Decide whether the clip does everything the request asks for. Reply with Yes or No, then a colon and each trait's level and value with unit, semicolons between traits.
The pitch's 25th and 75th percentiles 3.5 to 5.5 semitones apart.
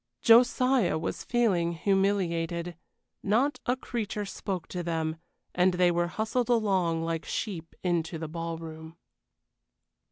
Yes: average, 4.3 semitones